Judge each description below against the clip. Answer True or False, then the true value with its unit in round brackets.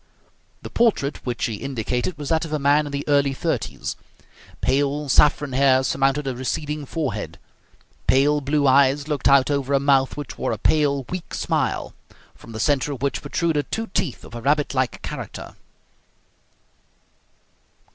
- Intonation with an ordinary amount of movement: False (2.0 semitones)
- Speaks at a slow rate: False (160 wpm)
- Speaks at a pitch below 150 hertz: True (140 Hz)